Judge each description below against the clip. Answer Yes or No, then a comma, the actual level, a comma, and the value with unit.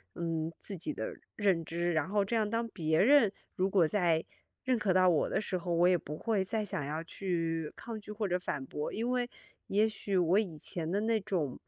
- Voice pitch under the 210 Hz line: Yes, medium, 185 Hz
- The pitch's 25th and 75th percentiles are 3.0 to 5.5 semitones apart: Yes, average, 4.3 semitones